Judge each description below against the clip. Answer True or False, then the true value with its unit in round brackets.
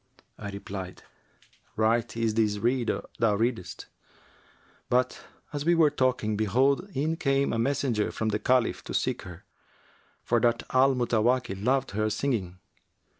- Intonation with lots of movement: False (3.6 semitones)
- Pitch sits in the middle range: False (115 Hz)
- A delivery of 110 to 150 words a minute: True (140 wpm)